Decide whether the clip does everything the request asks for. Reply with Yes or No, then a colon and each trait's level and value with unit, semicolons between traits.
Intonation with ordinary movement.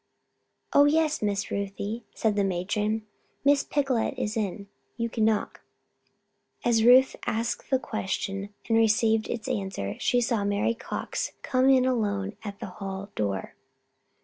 Yes: average, 3.1 semitones